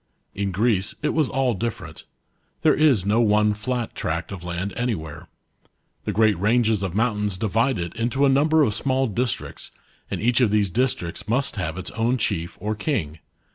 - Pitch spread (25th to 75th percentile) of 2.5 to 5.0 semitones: Yes, average, 4.2 semitones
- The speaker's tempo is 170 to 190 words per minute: Yes, average, 175 wpm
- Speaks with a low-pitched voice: Yes, low, 110 Hz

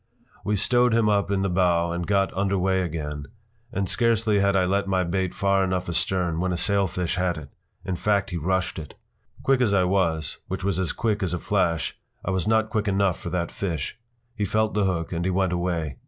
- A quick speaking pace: Yes, fast, 225 wpm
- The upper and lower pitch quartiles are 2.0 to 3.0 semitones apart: Yes, narrow, 2.5 semitones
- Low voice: Yes, very low, 95 Hz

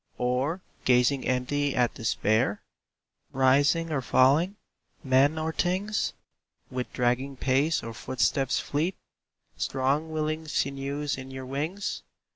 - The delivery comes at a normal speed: No, slow, 110 wpm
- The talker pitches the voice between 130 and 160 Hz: Yes, low, 135 Hz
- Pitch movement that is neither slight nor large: Yes, average, 3.3 semitones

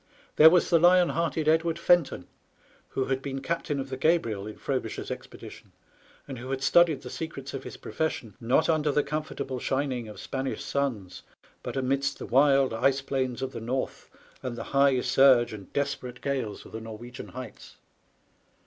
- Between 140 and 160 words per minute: No, average, 175 wpm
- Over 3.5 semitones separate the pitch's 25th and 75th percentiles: No, average, 3.0 semitones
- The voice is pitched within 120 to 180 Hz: Yes, low, 135 Hz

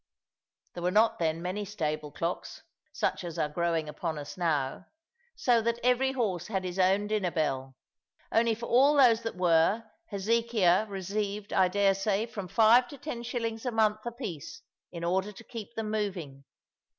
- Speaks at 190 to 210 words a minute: No, average, 165 wpm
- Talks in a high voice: Yes, high, 200 Hz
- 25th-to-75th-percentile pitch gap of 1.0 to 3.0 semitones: No, average, 4.8 semitones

